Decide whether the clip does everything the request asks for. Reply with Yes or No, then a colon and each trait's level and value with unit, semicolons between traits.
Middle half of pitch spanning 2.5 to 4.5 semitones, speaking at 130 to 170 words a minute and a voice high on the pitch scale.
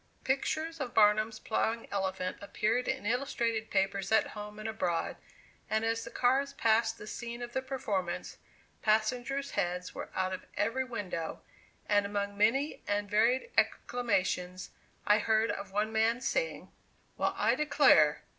Yes: average, 3.5 semitones; average, 145 wpm; high, 220 Hz